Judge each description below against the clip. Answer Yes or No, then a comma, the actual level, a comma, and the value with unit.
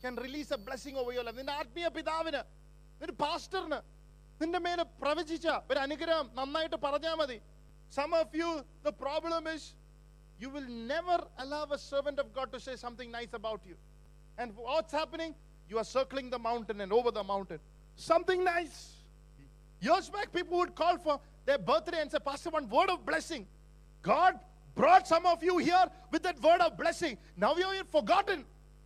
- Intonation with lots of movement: Yes, wide, 5.7 semitones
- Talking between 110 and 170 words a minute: Yes, average, 165 wpm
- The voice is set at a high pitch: Yes, very high, 290 Hz